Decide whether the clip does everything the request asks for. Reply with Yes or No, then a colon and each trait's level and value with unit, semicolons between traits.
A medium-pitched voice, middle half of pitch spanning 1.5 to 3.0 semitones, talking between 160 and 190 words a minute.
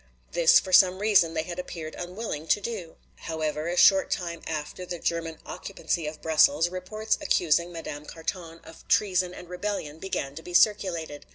Yes: medium, 170 Hz; narrow, 2.4 semitones; average, 170 wpm